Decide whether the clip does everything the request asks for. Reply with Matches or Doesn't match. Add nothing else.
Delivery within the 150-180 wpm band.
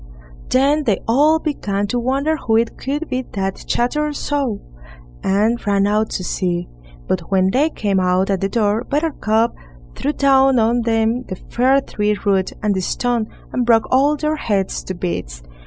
Matches